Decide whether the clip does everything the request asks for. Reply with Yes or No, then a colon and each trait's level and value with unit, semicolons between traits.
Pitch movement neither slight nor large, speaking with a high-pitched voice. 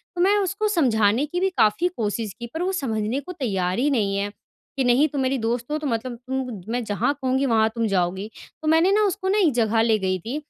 No: wide, 6.0 semitones; very high, 250 Hz